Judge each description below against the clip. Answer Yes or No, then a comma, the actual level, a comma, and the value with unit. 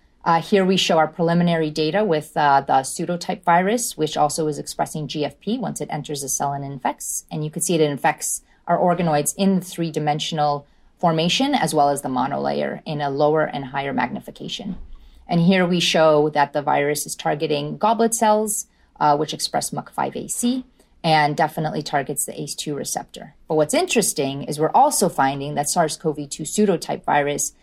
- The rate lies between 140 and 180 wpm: Yes, average, 170 wpm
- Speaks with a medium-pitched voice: Yes, medium, 155 Hz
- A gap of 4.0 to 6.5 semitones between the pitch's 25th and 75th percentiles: No, average, 3.4 semitones